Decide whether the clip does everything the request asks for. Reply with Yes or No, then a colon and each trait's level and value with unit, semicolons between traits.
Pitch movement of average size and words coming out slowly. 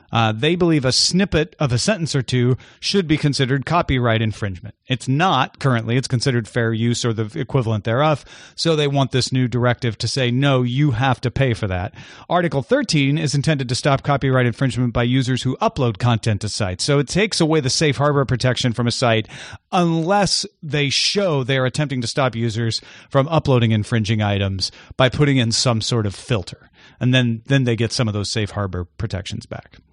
No: average, 3.8 semitones; average, 195 wpm